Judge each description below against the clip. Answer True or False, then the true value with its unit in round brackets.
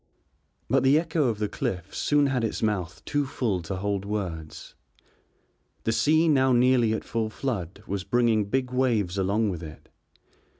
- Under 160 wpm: False (165 wpm)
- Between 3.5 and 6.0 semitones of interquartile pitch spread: True (5.1 semitones)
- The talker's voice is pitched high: False (110 Hz)